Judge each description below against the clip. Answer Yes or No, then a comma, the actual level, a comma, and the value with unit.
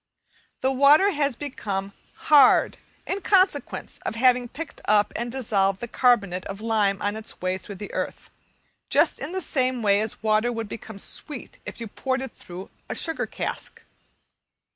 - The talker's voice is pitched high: Yes, high, 230 Hz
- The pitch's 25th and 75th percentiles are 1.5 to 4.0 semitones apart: No, average, 4.7 semitones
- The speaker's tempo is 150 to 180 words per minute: Yes, average, 165 wpm